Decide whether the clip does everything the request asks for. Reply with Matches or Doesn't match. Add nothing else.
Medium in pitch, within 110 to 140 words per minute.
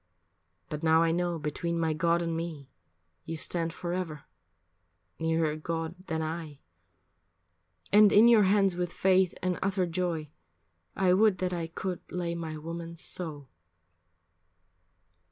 Matches